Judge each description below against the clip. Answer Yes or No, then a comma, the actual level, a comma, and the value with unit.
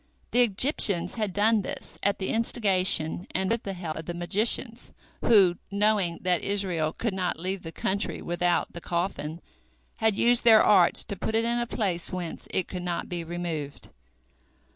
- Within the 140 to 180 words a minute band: Yes, average, 175 wpm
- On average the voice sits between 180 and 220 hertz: Yes, high, 190 Hz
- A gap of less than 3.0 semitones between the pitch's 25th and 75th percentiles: No, average, 3.7 semitones